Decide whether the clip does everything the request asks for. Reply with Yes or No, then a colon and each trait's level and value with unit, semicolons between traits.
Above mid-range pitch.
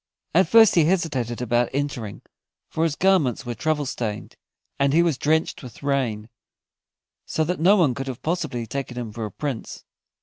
No: medium, 140 Hz